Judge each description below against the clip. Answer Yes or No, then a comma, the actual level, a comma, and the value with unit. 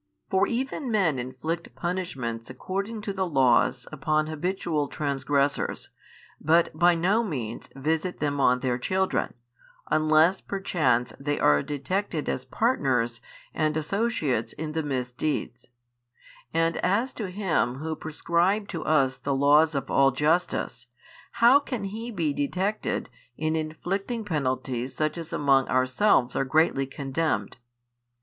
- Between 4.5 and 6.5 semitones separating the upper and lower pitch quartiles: Yes, wide, 5.5 semitones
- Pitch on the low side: No, medium, 155 Hz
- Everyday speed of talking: No, slow, 130 wpm